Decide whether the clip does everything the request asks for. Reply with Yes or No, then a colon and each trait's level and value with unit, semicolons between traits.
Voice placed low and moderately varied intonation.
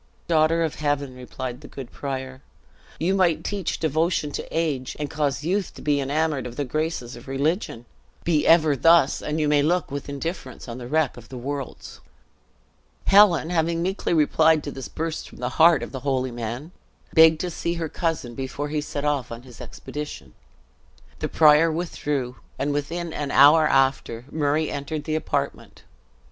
No: medium, 150 Hz; average, 3.3 semitones